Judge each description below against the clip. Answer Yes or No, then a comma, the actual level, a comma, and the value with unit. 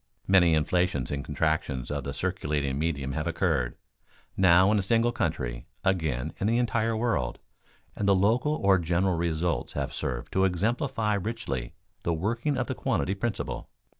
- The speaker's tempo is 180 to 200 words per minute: No, average, 160 wpm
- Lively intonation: Yes, wide, 6.2 semitones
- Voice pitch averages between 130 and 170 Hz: No, very low, 90 Hz